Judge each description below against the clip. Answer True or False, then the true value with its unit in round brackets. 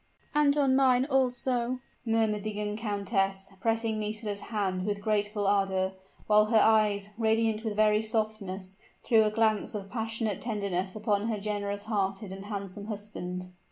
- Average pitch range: False (1.8 semitones)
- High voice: True (210 Hz)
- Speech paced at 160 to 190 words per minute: False (150 wpm)